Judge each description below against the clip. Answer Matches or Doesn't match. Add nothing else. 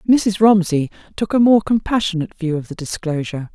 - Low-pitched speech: Doesn't match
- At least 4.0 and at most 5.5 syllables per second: Doesn't match